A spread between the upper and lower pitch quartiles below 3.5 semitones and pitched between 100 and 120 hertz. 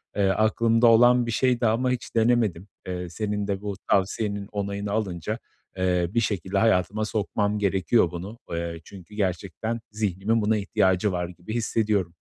Yes: average, 3.1 semitones; low, 105 Hz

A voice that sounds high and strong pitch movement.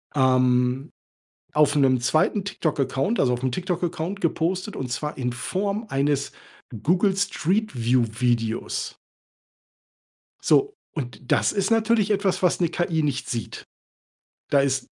No: medium, 150 Hz; wide, 6.8 semitones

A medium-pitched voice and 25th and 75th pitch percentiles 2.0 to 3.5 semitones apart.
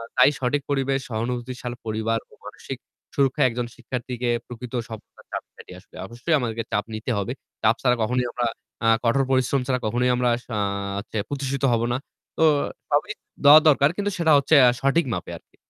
No: low, 125 Hz; average, 2.8 semitones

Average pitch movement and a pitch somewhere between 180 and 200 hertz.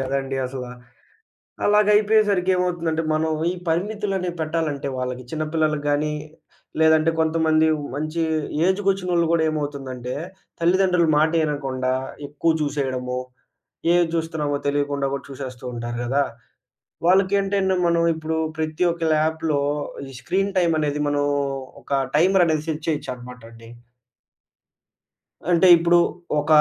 No: average, 3.6 semitones; medium, 155 Hz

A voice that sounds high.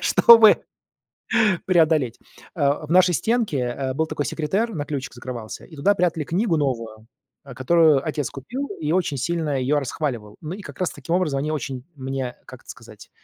No: medium, 150 Hz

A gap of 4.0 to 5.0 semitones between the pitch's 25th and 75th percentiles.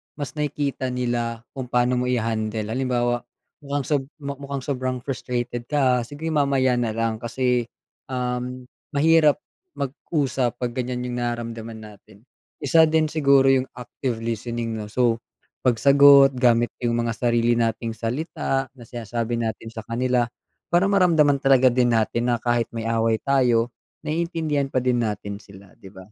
No: average, 2.9 semitones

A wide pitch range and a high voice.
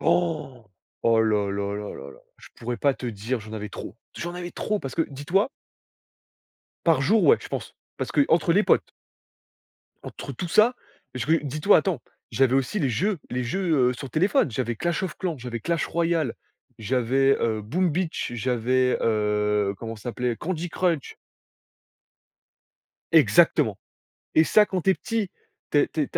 No: wide, 6.9 semitones; low, 135 Hz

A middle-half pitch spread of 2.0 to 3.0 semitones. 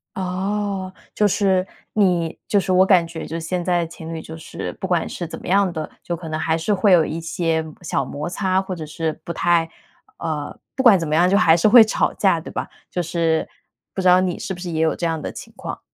Yes: narrow, 2.6 semitones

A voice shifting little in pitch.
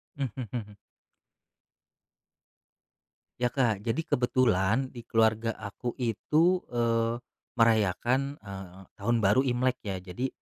No: average, 3.6 semitones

